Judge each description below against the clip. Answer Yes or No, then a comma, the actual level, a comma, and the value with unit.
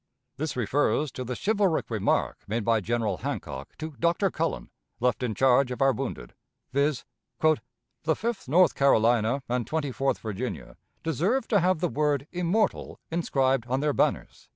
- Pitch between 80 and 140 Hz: Yes, low, 135 Hz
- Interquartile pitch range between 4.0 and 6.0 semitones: Yes, average, 4.9 semitones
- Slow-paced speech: No, average, 155 wpm